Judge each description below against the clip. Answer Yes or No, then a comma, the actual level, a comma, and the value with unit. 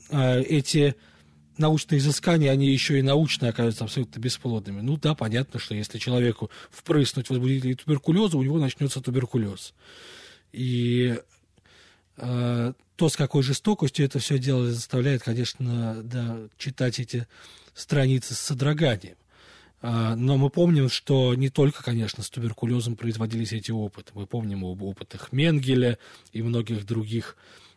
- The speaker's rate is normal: Yes, average, 130 wpm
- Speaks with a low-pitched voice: Yes, low, 125 Hz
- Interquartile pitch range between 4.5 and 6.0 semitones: No, average, 3.4 semitones